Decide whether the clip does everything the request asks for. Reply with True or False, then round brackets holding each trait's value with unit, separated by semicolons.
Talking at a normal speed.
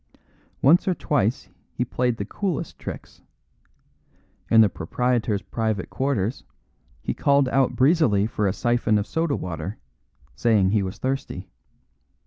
False (130 wpm)